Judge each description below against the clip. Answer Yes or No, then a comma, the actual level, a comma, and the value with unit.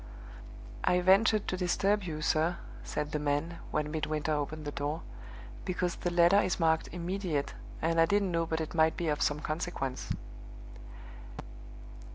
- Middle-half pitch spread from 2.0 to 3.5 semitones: Yes, average, 2.8 semitones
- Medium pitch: Yes, medium, 165 Hz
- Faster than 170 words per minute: No, average, 155 wpm